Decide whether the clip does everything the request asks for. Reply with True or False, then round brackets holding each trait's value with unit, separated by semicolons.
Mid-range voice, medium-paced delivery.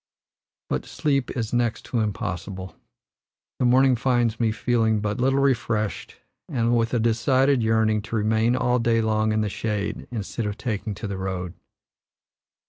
False (115 Hz; 155 wpm)